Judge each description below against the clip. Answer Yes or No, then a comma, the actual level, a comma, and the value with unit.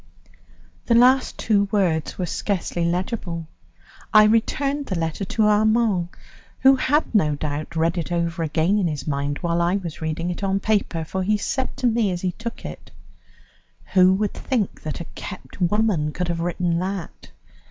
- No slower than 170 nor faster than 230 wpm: Yes, average, 175 wpm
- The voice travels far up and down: No, average, 4.3 semitones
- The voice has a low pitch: No, medium, 185 Hz